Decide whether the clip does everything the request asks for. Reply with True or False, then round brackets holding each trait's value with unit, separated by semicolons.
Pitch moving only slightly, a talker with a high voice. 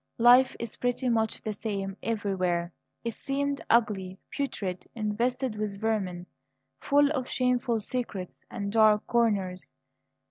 False (3.9 semitones; 220 Hz)